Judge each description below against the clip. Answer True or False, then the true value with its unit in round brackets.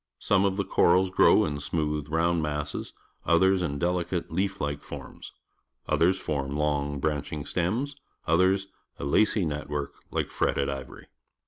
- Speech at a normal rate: True (155 wpm)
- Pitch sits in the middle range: False (80 Hz)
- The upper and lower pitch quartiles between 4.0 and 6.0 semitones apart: True (4.3 semitones)